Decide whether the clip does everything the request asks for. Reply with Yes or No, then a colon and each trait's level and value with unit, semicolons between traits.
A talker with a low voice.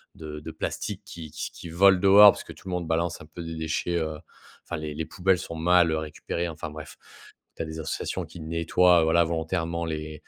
Yes: very low, 80 Hz